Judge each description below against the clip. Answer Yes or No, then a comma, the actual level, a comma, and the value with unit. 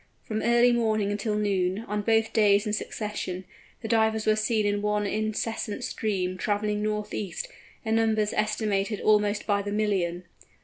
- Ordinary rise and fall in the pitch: No, narrow, 1.1 semitones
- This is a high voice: Yes, high, 210 Hz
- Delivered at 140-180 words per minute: Yes, average, 160 wpm